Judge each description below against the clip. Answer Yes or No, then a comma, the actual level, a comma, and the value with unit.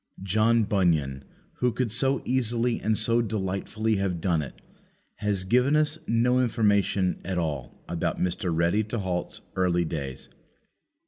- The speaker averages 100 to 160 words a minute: Yes, average, 140 wpm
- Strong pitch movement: No, average, 4.8 semitones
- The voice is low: Yes, low, 100 Hz